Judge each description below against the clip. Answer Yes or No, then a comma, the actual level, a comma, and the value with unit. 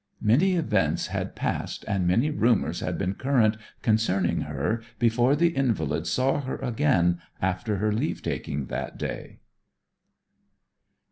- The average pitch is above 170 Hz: No, low, 110 Hz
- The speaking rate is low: Yes, slow, 130 wpm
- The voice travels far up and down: Yes, wide, 6.3 semitones